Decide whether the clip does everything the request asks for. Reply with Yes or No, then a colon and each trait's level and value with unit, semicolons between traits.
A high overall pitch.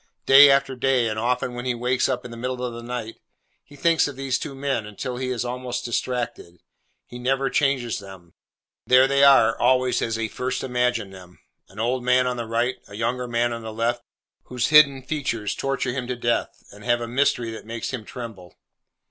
No: low, 125 Hz